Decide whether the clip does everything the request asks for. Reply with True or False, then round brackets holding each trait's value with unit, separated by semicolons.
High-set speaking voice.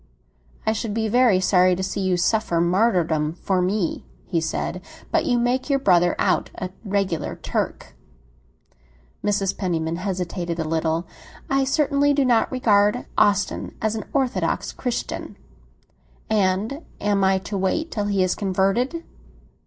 True (200 Hz)